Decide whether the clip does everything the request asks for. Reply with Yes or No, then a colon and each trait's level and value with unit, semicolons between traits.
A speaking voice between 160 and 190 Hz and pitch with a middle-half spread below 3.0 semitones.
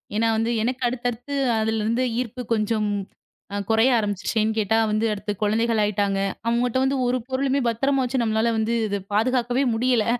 No: high, 230 Hz; narrow, 2.6 semitones